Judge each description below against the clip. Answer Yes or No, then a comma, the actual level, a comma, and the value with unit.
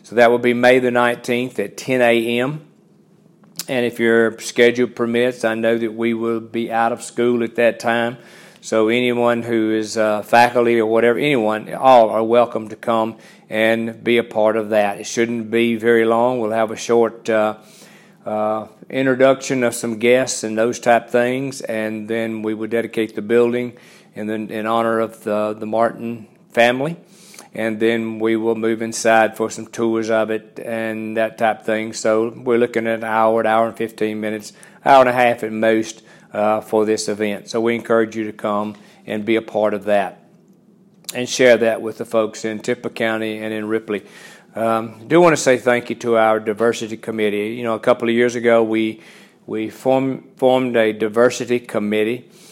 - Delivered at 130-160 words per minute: No, average, 195 wpm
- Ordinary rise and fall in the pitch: No, narrow, 1.7 semitones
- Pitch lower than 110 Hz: No, low, 115 Hz